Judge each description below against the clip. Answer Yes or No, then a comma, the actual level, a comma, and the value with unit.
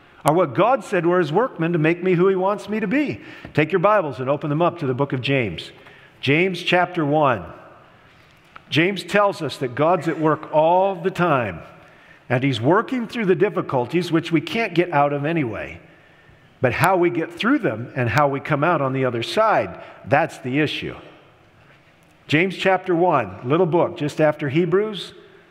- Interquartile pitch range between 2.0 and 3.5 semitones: No, average, 4.6 semitones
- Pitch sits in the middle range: Yes, medium, 170 Hz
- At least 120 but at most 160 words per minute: No, average, 190 wpm